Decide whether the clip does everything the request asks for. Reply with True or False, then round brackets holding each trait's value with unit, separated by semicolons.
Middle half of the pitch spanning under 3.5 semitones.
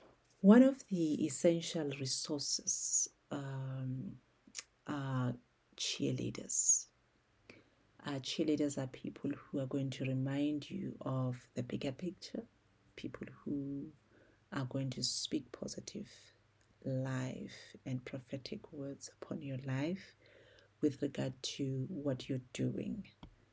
True (2.4 semitones)